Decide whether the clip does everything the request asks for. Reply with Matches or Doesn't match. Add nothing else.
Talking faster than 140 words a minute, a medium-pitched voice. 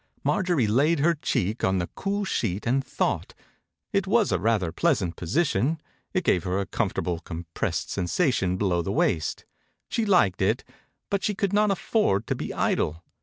Doesn't match